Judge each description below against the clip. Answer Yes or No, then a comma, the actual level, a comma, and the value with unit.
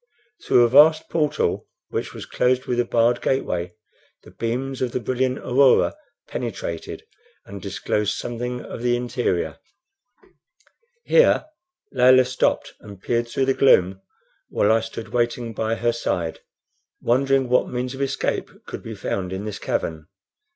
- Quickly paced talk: No, average, 145 wpm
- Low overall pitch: Yes, low, 120 Hz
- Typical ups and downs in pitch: Yes, average, 3.0 semitones